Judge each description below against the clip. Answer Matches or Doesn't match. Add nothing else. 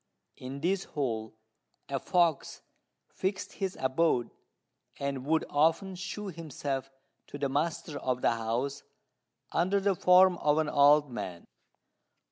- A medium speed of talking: Doesn't match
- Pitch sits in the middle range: Matches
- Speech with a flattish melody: Doesn't match